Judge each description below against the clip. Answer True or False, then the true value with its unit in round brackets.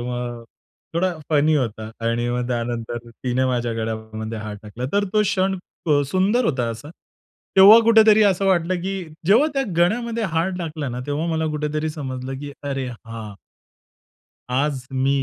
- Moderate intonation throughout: False (7.5 semitones)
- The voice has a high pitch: False (140 Hz)